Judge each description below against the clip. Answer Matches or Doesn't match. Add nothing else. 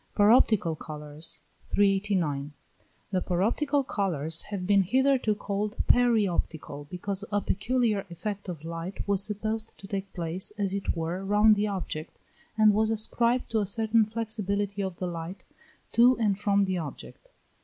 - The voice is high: Matches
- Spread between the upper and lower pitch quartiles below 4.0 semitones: Matches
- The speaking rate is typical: Matches